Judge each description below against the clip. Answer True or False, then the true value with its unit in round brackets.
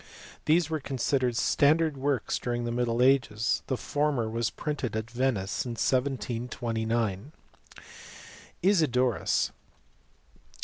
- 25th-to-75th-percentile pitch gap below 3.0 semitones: False (3.4 semitones)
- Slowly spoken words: True (100 wpm)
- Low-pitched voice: True (125 Hz)